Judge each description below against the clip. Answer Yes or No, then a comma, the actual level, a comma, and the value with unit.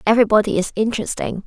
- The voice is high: Yes, high, 215 Hz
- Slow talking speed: Yes, slow, 125 wpm